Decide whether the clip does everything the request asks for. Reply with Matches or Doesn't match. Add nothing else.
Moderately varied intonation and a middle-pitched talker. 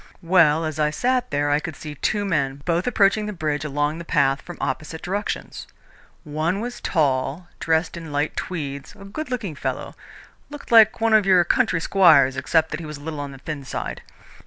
Matches